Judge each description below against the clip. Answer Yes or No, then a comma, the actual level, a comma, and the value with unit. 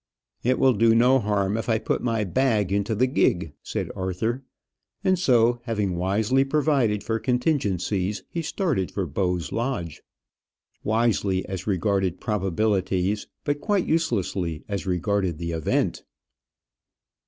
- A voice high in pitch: No, low, 105 Hz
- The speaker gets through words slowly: Yes, slow, 130 wpm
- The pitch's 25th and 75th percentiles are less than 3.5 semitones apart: No, average, 4.7 semitones